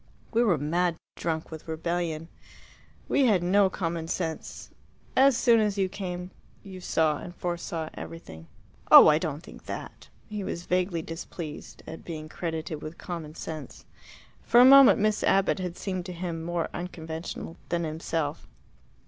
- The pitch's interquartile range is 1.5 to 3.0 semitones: Yes, average, 2.7 semitones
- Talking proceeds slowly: No, average, 155 wpm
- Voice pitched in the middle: Yes, medium, 170 Hz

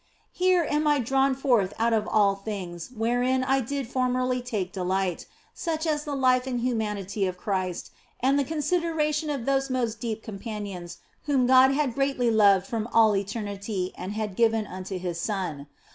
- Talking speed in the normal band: Yes, average, 175 wpm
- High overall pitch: Yes, high, 230 Hz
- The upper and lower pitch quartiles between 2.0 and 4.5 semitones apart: No, average, 5.2 semitones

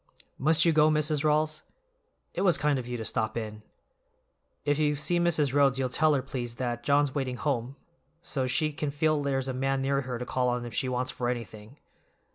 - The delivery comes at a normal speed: No, fast, 210 wpm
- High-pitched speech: No, low, 135 Hz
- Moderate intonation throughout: Yes, average, 3.3 semitones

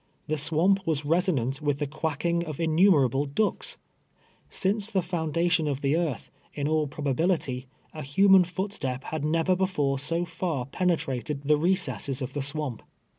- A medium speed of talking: Yes, average, 155 wpm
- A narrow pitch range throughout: No, average, 3.8 semitones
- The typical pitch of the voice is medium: Yes, medium, 155 Hz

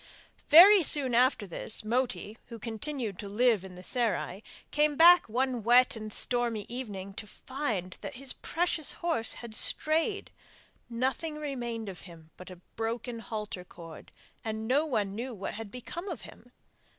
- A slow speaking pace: No, average, 160 wpm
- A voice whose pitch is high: Yes, high, 235 Hz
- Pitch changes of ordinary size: Yes, average, 4.4 semitones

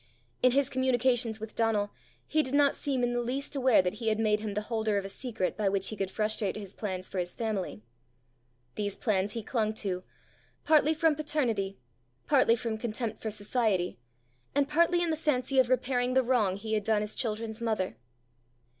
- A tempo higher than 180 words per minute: Yes, average, 195 wpm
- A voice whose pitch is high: Yes, high, 225 Hz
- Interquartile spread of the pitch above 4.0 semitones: No, average, 3.7 semitones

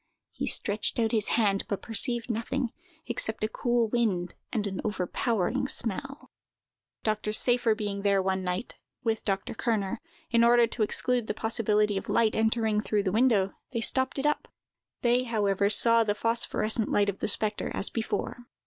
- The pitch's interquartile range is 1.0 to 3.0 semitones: Yes, narrow, 2.5 semitones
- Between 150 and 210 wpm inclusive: Yes, average, 165 wpm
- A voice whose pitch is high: Yes, high, 220 Hz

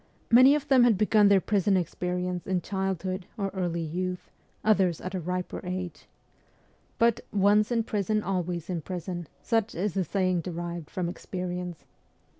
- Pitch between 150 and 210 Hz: Yes, medium, 185 Hz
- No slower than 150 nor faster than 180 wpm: Yes, average, 155 wpm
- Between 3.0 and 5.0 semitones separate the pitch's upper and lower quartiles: No, narrow, 2.5 semitones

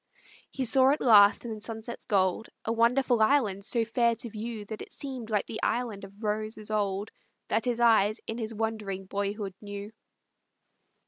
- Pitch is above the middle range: Yes, high, 220 Hz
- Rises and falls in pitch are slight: Yes, narrow, 2.3 semitones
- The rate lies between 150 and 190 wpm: Yes, average, 175 wpm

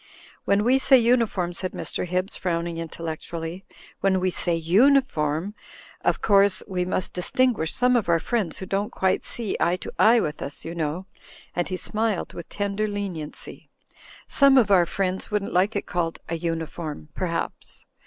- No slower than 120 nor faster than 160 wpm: No, average, 175 wpm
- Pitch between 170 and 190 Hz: Yes, medium, 185 Hz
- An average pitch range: Yes, average, 3.8 semitones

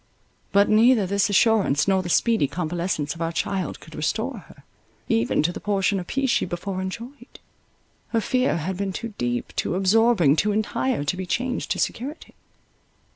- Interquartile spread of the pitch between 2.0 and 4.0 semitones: No, average, 4.5 semitones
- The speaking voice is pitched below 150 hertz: No, high, 195 Hz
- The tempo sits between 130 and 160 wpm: No, average, 175 wpm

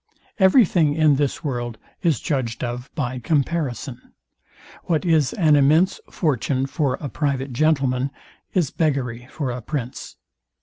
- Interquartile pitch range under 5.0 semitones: Yes, average, 3.8 semitones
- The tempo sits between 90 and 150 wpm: Yes, slow, 135 wpm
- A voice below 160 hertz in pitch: Yes, medium, 140 Hz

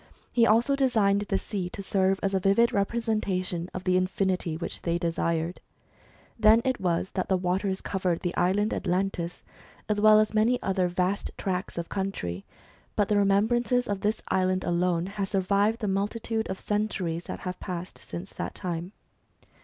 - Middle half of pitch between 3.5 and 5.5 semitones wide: No, average, 2.7 semitones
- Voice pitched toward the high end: Yes, high, 195 Hz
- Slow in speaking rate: No, average, 175 wpm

